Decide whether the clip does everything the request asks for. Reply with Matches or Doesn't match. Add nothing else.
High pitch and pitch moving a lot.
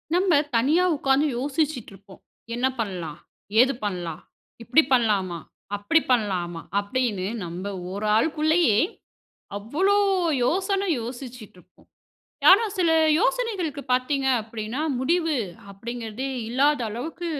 Matches